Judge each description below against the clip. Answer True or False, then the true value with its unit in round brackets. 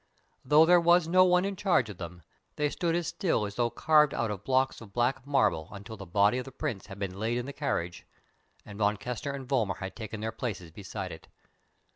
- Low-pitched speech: True (120 Hz)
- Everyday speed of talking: False (225 wpm)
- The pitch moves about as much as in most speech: False (6.5 semitones)